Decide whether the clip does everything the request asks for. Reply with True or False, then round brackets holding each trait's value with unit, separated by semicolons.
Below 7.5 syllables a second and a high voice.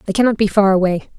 False (7.9 syllables/s; 200 Hz)